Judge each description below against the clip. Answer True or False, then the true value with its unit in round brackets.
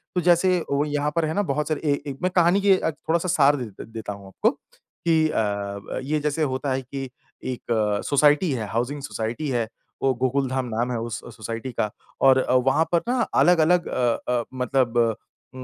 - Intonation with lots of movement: False (4.6 semitones)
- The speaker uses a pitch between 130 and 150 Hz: True (135 Hz)